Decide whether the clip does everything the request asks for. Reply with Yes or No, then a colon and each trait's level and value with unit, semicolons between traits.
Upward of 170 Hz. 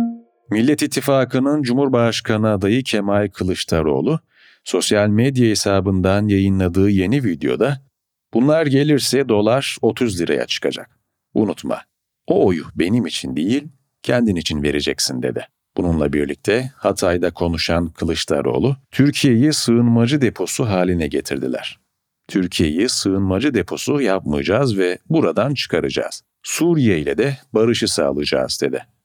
No: low, 110 Hz